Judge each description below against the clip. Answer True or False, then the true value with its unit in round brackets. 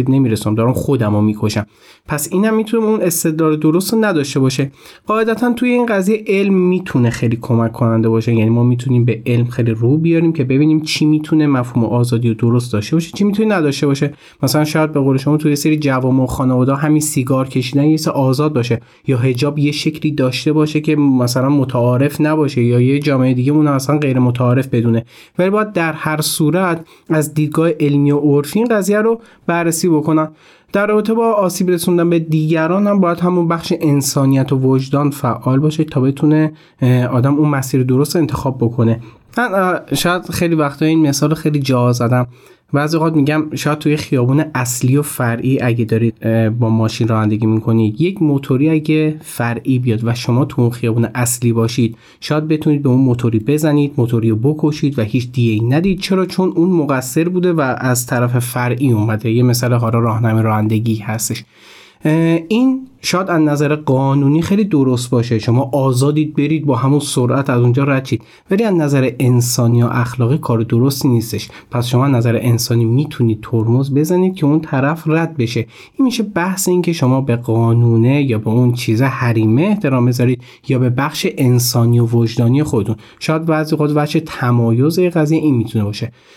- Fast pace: True (180 wpm)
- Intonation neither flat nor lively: True (4.4 semitones)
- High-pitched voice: False (140 Hz)